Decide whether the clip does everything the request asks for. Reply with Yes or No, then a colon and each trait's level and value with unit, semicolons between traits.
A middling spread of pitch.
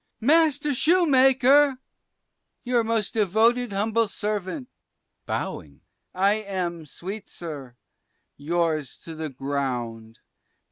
No: wide, 7.9 semitones